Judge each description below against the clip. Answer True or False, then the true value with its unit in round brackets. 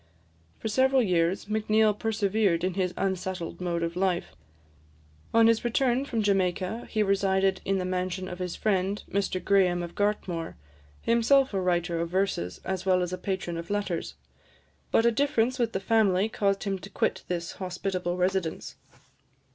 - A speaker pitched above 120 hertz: True (190 Hz)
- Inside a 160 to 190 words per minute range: True (165 wpm)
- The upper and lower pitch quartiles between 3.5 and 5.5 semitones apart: False (3.0 semitones)